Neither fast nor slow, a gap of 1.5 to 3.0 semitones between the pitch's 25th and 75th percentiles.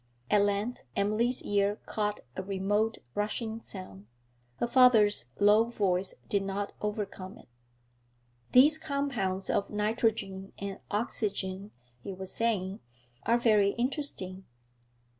No: slow, 115 wpm; average, 2.7 semitones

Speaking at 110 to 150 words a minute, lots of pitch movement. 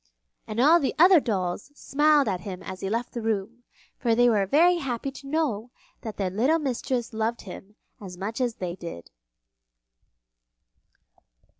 No: average, 160 wpm; wide, 5.7 semitones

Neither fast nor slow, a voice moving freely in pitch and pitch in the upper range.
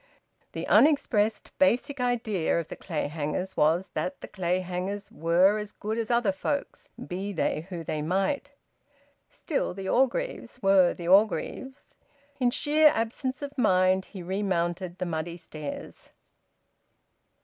No: slow, 130 wpm; wide, 5.7 semitones; high, 195 Hz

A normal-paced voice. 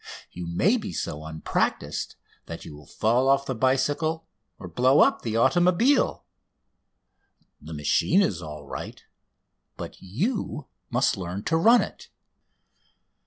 No: slow, 130 wpm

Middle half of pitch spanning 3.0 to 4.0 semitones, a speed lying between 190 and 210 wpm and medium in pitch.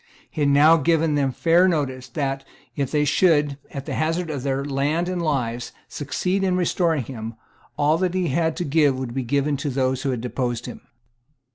Yes: average, 3.7 semitones; average, 200 wpm; medium, 145 Hz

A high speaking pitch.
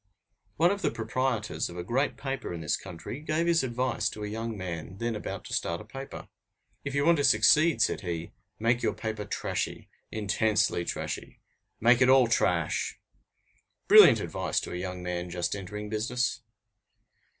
No: low, 110 Hz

